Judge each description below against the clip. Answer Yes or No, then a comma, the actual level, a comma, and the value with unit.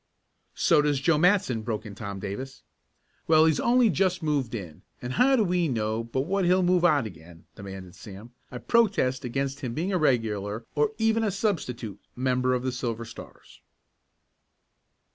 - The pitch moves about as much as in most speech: No, wide, 7.9 semitones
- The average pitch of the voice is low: Yes, low, 130 Hz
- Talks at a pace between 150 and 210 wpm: Yes, average, 170 wpm